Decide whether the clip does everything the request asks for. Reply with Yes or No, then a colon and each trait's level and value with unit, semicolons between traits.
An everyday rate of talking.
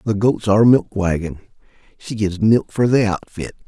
Yes: average, 165 wpm